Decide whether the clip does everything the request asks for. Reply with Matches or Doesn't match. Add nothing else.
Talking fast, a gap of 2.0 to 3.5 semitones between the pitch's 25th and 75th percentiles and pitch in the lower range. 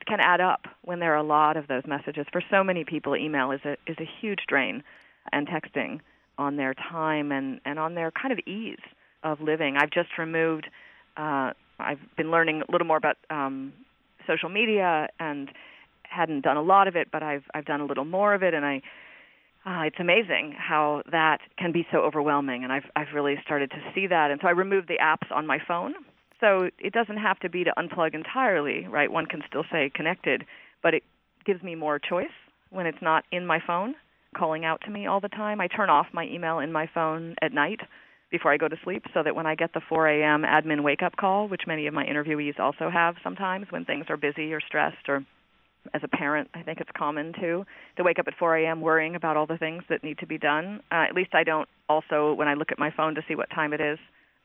Doesn't match